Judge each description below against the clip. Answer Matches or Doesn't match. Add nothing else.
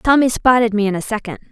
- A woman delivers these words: Matches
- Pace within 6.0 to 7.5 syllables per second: Matches